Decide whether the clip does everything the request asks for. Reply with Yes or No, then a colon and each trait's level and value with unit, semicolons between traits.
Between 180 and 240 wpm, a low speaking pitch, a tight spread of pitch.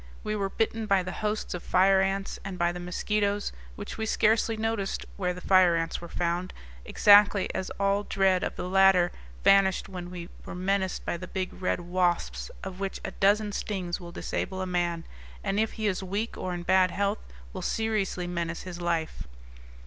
No: average, 190 wpm; high, 190 Hz; narrow, 2.2 semitones